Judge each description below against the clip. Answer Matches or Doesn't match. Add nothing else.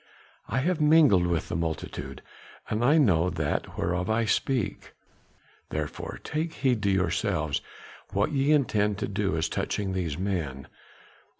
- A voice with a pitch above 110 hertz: Doesn't match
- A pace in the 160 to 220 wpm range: Doesn't match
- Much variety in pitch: Matches